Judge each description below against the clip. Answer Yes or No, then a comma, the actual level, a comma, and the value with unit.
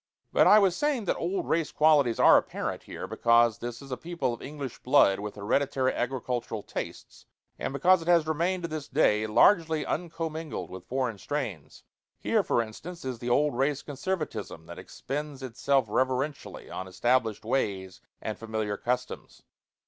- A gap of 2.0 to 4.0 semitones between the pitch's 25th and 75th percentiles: No, wide, 5.5 semitones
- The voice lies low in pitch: Yes, low, 130 Hz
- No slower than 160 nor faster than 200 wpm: Yes, average, 165 wpm